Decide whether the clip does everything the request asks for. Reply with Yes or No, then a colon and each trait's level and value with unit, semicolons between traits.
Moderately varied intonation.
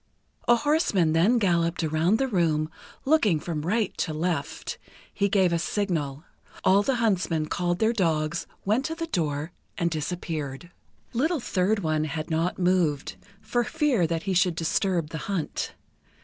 Yes: average, 4.7 semitones